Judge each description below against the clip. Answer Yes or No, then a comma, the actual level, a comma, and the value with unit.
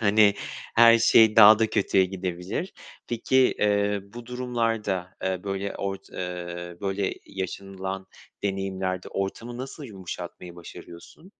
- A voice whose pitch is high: No, low, 100 Hz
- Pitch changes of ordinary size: Yes, average, 3.2 semitones